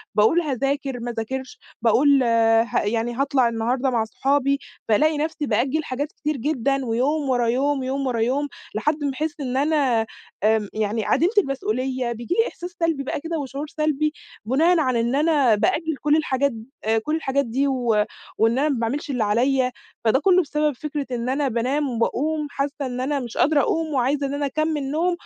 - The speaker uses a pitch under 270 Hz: No, very high, 275 Hz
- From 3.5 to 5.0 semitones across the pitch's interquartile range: Yes, average, 3.8 semitones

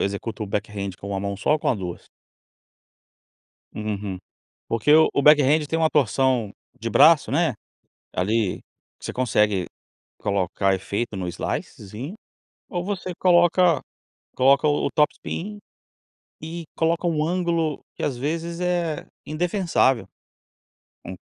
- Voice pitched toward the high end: No, medium, 140 Hz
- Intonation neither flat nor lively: No, wide, 8.0 semitones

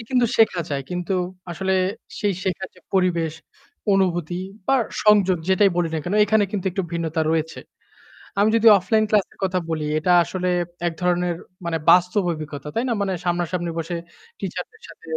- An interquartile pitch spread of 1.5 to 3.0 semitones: Yes, narrow, 2.6 semitones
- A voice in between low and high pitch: Yes, medium, 180 Hz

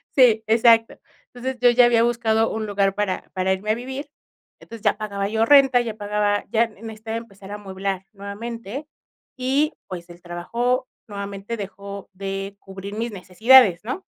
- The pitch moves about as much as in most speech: Yes, average, 3.0 semitones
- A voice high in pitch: Yes, high, 215 Hz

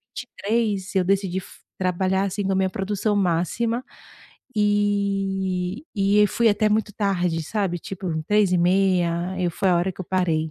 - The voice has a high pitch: Yes, high, 195 Hz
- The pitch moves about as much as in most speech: No, narrow, 2.2 semitones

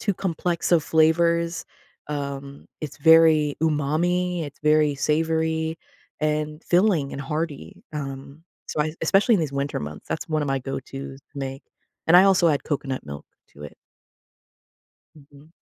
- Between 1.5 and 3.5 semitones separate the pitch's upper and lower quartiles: Yes, average, 2.7 semitones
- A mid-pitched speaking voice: Yes, medium, 150 Hz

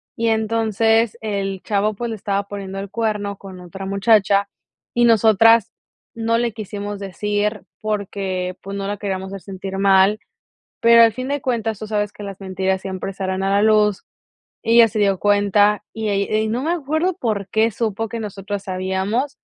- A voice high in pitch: Yes, high, 205 Hz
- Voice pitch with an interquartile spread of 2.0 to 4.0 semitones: Yes, narrow, 2.4 semitones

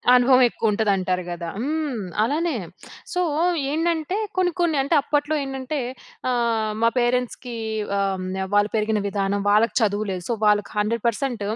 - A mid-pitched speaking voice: No, high, 235 Hz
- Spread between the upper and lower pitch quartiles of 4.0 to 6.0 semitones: Yes, wide, 5.4 semitones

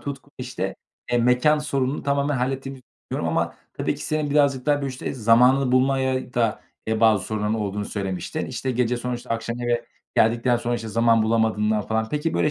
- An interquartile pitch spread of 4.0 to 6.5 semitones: No, average, 3.3 semitones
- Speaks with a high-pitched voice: No, low, 120 Hz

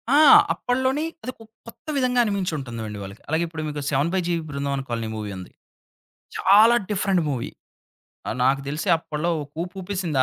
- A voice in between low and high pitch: Yes, medium, 160 Hz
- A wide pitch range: Yes, wide, 6.7 semitones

